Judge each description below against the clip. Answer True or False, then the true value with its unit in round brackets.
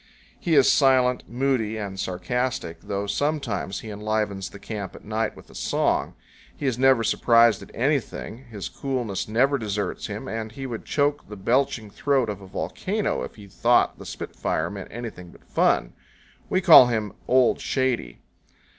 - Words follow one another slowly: False (165 wpm)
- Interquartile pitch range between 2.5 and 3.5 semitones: False (4.4 semitones)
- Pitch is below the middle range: True (115 Hz)